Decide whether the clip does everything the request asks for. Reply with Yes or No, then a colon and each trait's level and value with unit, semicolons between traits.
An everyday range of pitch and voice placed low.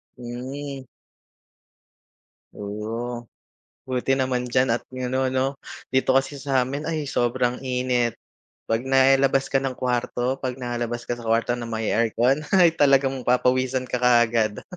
No: narrow, 1.9 semitones; low, 125 Hz